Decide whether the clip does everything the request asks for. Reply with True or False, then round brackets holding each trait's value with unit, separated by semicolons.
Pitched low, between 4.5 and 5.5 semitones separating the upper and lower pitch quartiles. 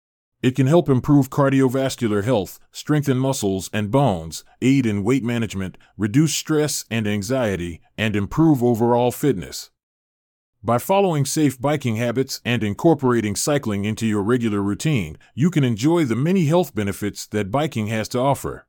True (120 Hz; 5.2 semitones)